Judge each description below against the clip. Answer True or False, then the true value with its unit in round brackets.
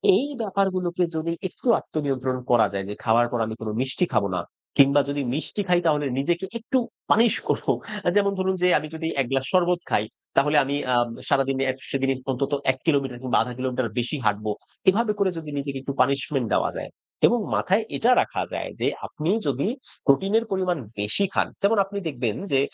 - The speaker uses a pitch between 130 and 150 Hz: True (140 Hz)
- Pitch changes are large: True (6.1 semitones)